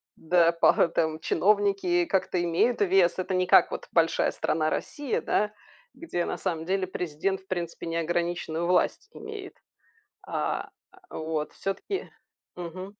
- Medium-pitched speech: Yes, medium, 180 Hz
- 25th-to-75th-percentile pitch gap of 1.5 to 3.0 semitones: Yes, average, 2.7 semitones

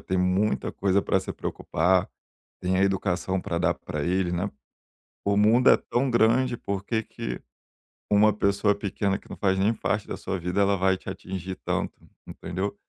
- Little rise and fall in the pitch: Yes, narrow, 2.0 semitones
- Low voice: Yes, very low, 95 Hz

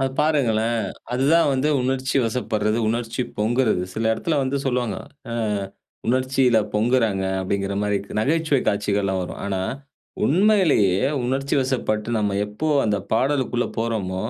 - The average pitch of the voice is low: Yes, low, 120 Hz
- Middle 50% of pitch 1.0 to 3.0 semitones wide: No, average, 4.2 semitones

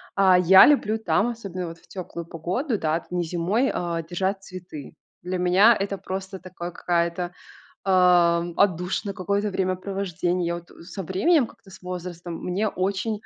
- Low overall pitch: No, medium, 185 Hz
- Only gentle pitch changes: Yes, narrow, 2.2 semitones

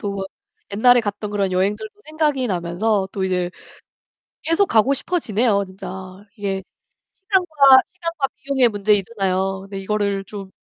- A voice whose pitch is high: Yes, high, 205 Hz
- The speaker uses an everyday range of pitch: Yes, average, 5.0 semitones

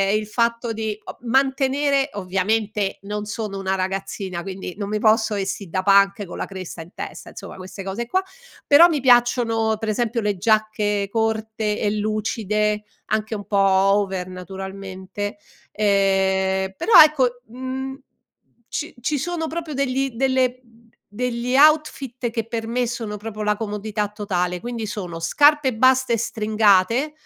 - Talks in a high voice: Yes, high, 215 Hz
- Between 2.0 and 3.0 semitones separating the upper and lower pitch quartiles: No, average, 3.8 semitones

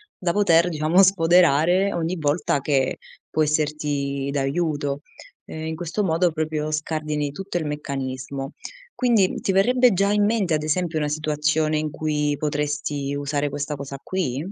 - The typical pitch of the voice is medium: Yes, medium, 155 Hz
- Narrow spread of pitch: No, average, 3.2 semitones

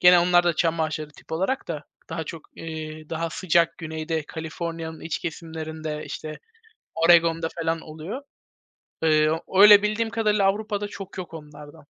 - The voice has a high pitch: No, medium, 165 Hz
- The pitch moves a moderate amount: No, narrow, 2.2 semitones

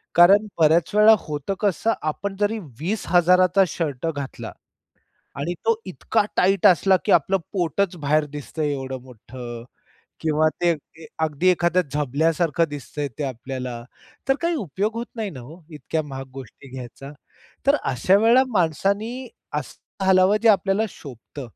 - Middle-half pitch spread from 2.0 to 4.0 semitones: No, wide, 5.6 semitones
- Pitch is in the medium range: Yes, medium, 165 Hz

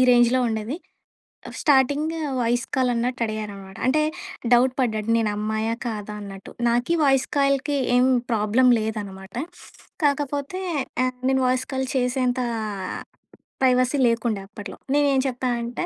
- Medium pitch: No, high, 245 Hz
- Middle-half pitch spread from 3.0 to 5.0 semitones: Yes, average, 3.3 semitones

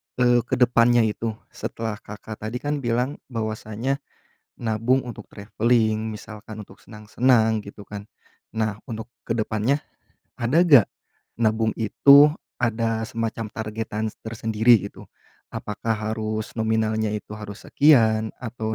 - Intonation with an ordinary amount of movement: No, narrow, 1.8 semitones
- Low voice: Yes, low, 110 Hz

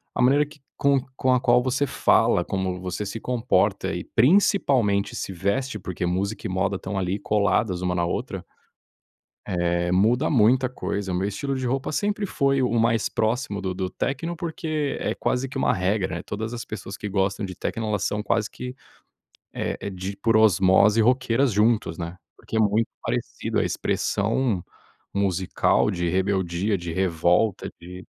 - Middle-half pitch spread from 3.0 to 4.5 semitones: No, average, 5.1 semitones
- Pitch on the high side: No, low, 105 Hz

